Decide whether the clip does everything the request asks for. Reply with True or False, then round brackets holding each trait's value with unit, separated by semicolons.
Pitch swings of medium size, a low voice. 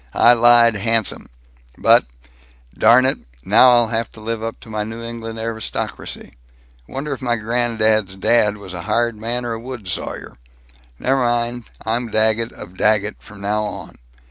False (1.8 semitones; 115 Hz)